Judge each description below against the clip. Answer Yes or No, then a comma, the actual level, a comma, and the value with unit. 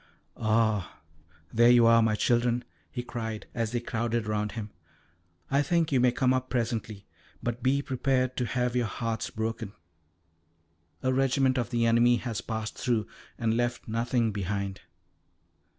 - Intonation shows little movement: Yes, narrow, 2.0 semitones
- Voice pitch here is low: Yes, low, 120 Hz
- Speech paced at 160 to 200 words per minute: No, average, 150 wpm